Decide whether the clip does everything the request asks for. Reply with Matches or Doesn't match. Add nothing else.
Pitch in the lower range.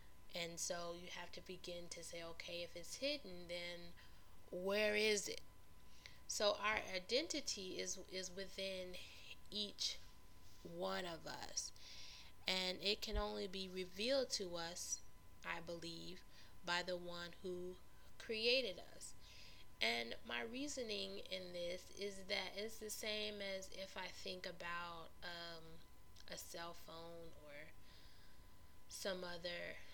Doesn't match